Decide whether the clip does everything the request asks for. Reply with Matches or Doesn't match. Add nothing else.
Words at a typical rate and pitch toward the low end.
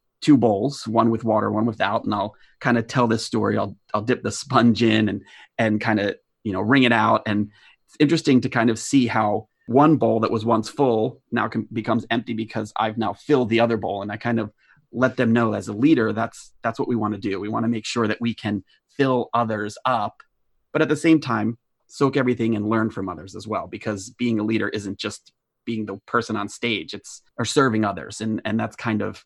Doesn't match